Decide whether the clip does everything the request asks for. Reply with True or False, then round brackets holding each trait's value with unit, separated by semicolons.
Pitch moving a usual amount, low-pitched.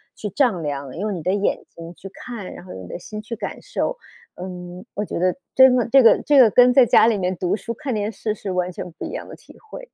False (4.9 semitones; 205 Hz)